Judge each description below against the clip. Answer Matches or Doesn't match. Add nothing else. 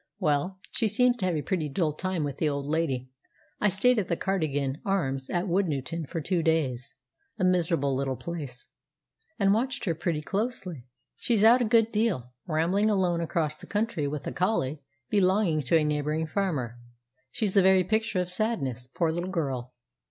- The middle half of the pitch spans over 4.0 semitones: Matches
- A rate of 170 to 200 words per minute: Matches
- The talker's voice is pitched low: Doesn't match